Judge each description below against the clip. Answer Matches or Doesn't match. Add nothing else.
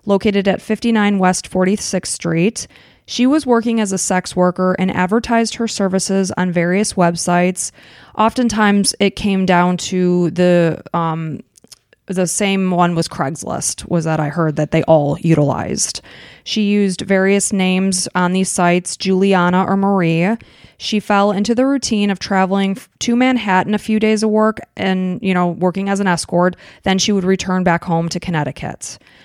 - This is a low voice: Doesn't match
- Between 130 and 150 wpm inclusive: Doesn't match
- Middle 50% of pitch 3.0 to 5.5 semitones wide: Doesn't match